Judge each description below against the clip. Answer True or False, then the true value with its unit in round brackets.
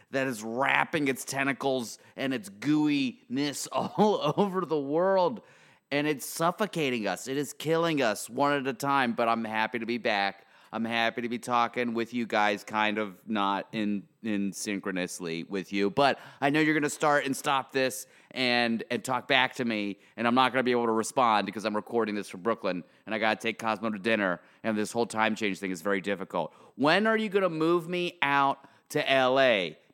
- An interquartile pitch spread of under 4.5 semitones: False (4.8 semitones)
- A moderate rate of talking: False (210 wpm)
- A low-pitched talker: True (125 Hz)